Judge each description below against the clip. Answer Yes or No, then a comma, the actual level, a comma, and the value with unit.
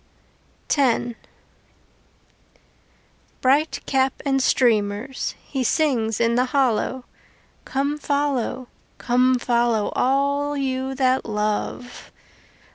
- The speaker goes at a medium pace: No, slow, 85 wpm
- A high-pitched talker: Yes, very high, 260 Hz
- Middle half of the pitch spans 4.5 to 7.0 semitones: No, narrow, 2.4 semitones